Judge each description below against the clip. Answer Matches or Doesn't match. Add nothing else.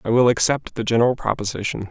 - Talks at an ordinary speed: Matches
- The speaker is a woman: Doesn't match